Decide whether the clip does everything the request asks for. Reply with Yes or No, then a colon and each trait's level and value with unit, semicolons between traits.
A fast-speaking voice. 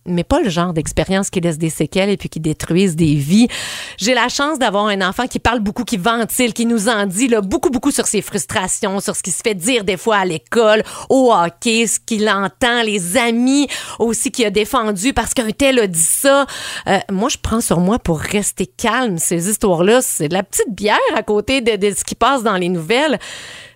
Yes: fast, 225 wpm